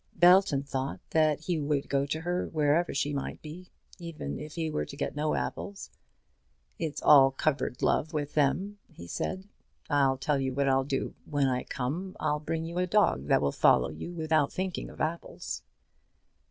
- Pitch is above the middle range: No, medium, 150 Hz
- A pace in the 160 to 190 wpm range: Yes, average, 180 wpm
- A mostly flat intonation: No, average, 3.5 semitones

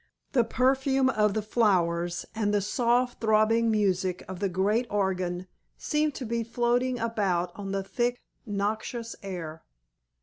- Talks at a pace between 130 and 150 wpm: Yes, average, 140 wpm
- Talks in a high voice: Yes, high, 215 Hz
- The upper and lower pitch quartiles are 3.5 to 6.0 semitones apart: Yes, average, 3.9 semitones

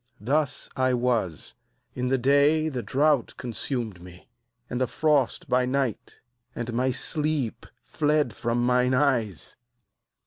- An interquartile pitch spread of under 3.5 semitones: Yes, average, 3.1 semitones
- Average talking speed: No, slow, 130 wpm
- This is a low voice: Yes, low, 125 Hz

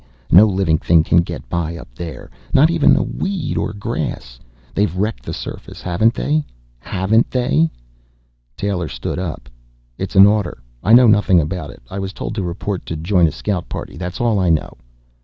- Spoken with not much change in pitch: No, average, 4.2 semitones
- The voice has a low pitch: Yes, very low, 95 Hz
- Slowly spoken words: No, average, 185 wpm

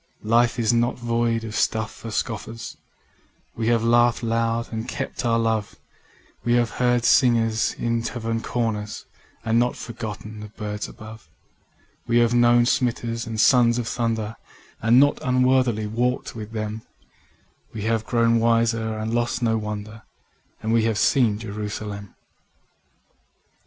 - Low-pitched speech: Yes, low, 115 Hz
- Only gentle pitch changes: Yes, narrow, 1.5 semitones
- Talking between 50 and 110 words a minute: No, average, 140 wpm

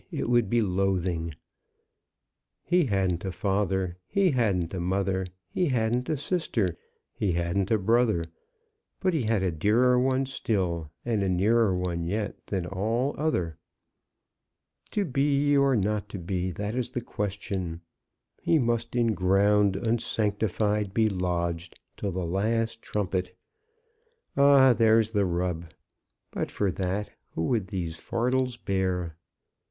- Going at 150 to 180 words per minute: No, slow, 135 wpm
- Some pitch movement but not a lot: Yes, average, 4.4 semitones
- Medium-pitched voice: No, low, 100 Hz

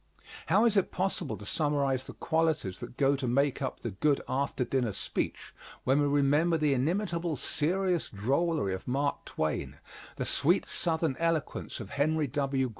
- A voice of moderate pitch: Yes, medium, 145 Hz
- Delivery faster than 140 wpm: Yes, average, 165 wpm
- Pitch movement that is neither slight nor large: Yes, average, 3.8 semitones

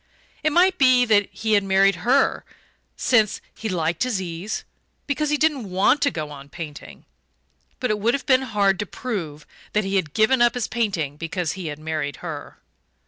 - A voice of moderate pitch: No, high, 205 Hz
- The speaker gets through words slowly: No, average, 190 wpm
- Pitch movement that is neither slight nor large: No, wide, 7.0 semitones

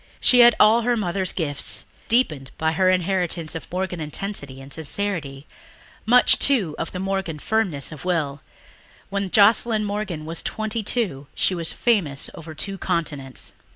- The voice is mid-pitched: Yes, medium, 180 Hz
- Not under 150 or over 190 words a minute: Yes, average, 155 wpm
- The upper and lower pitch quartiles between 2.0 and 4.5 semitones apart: No, average, 5.3 semitones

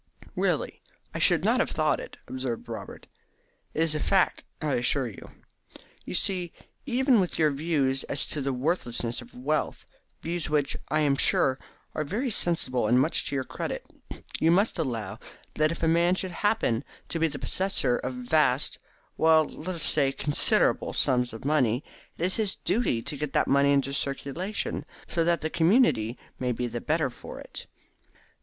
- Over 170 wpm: Yes, average, 180 wpm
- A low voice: No, medium, 150 Hz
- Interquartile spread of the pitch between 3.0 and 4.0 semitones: No, average, 4.7 semitones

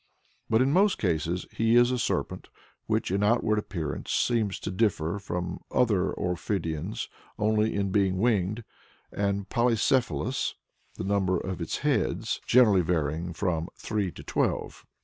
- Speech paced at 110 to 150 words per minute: Yes, average, 140 wpm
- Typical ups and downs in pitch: Yes, average, 4.0 semitones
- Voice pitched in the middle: No, low, 100 Hz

